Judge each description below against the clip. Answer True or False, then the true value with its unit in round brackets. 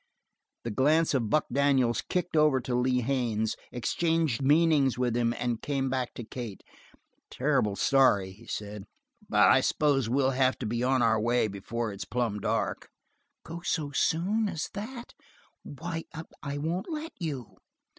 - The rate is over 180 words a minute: False (155 wpm)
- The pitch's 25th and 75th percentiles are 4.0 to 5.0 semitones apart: True (4.7 semitones)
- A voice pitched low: True (130 Hz)